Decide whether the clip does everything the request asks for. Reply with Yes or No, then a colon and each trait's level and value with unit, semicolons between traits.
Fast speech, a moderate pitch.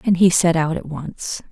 Yes: fast, 240 wpm; medium, 170 Hz